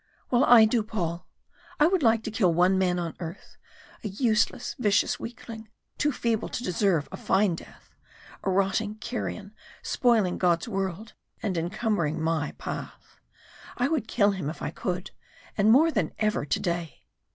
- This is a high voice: Yes, high, 205 Hz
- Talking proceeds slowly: No, average, 160 wpm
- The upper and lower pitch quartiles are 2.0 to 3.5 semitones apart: No, average, 4.3 semitones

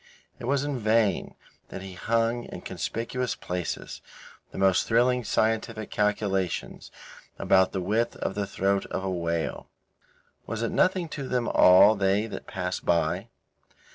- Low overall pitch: Yes, low, 105 Hz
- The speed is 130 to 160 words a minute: Yes, average, 145 wpm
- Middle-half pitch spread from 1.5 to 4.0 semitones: Yes, average, 3.6 semitones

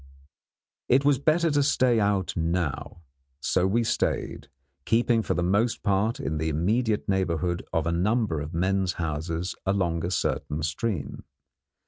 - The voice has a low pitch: Yes, very low, 95 Hz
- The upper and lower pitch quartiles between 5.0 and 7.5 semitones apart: Yes, wide, 5.4 semitones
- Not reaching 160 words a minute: Yes, average, 145 wpm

